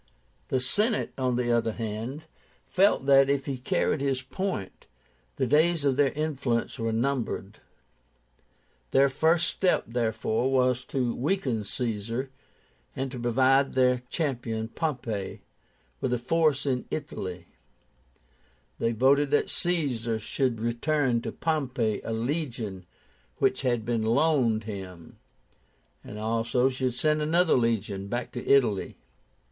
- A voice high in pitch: No, low, 125 Hz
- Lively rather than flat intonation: No, average, 3.6 semitones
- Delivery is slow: Yes, slow, 130 wpm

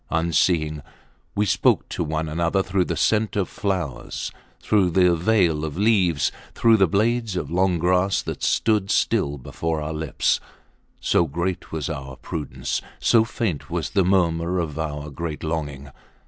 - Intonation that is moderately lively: Yes, average, 3.9 semitones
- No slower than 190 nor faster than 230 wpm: No, average, 155 wpm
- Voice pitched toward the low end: Yes, very low, 85 Hz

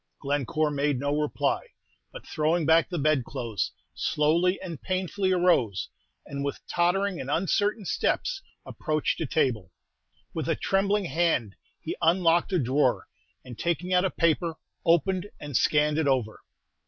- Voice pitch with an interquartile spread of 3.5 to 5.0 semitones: Yes, average, 4.2 semitones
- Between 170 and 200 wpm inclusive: No, average, 140 wpm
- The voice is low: No, medium, 160 Hz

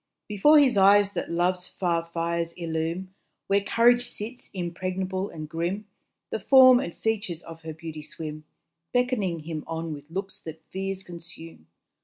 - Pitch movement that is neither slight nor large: Yes, average, 3.5 semitones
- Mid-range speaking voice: Yes, medium, 180 Hz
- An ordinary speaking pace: Yes, average, 150 wpm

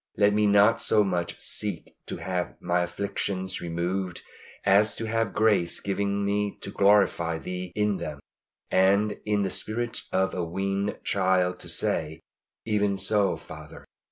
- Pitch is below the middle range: Yes, low, 100 Hz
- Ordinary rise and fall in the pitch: No, narrow, 2.3 semitones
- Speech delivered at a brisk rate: No, average, 150 wpm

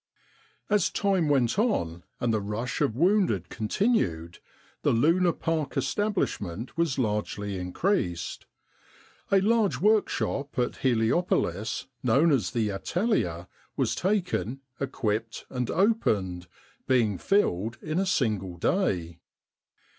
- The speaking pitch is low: Yes, low, 125 Hz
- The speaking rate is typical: No, slow, 115 wpm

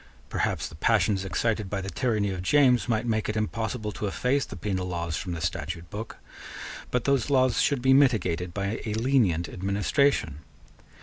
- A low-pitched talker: Yes, low, 105 Hz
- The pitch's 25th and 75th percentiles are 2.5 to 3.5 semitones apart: No, average, 5.1 semitones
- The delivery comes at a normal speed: Yes, average, 175 wpm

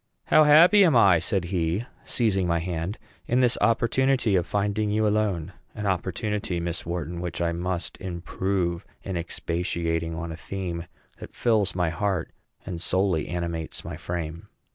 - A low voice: Yes, very low, 90 Hz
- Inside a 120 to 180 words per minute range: Yes, average, 155 wpm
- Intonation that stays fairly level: No, average, 3.6 semitones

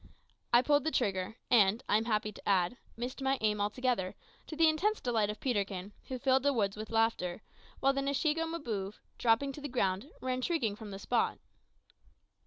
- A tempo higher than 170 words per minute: Yes, average, 190 wpm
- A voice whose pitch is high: Yes, high, 235 Hz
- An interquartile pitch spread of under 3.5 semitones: No, average, 4.9 semitones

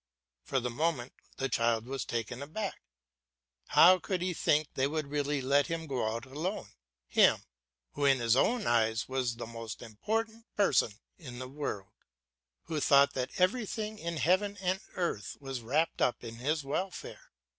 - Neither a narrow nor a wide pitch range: No, wide, 6.2 semitones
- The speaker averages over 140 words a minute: Yes, average, 165 wpm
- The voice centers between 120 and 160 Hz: Yes, medium, 140 Hz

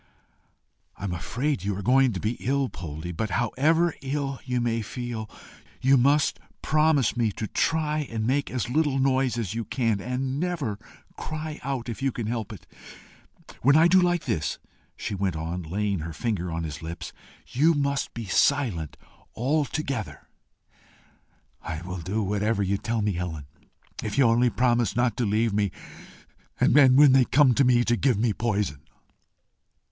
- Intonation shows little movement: No, average, 5.3 semitones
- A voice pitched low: Yes, low, 120 Hz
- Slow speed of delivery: No, average, 170 wpm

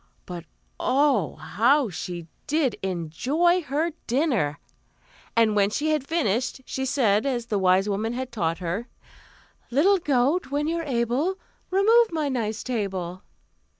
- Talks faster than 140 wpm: No, slow, 135 wpm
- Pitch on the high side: Yes, high, 245 Hz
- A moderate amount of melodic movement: No, wide, 7.0 semitones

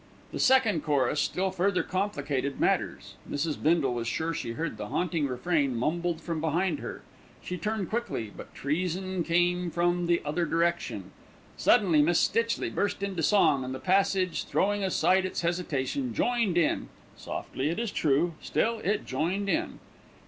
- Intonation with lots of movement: No, average, 4.3 semitones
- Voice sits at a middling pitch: Yes, medium, 175 Hz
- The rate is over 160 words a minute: No, average, 155 wpm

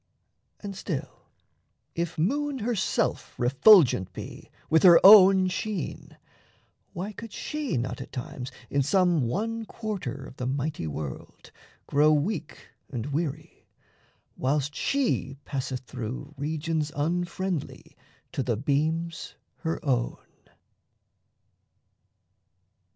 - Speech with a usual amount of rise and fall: No, wide, 6.0 semitones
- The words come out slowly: Yes, slow, 105 wpm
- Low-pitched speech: No, medium, 155 Hz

